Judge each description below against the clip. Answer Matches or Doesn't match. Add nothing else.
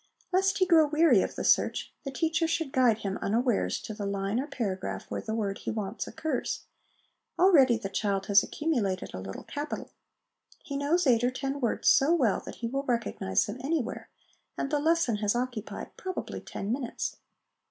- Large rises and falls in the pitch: Matches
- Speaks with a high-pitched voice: Matches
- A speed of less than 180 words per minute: Doesn't match